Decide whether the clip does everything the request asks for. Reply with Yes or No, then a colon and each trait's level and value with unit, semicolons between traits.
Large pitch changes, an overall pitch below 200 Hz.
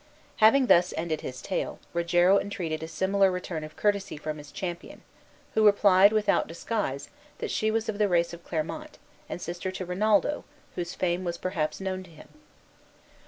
No: average, 3.1 semitones; medium, 185 Hz